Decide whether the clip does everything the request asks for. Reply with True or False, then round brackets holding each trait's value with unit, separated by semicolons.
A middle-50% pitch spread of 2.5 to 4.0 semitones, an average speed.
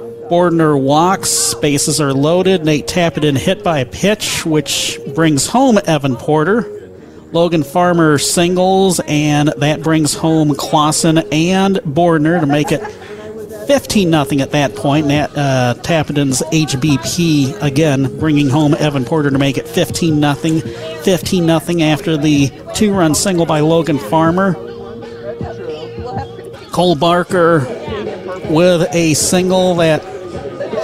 False (3.1 semitones; 115 wpm)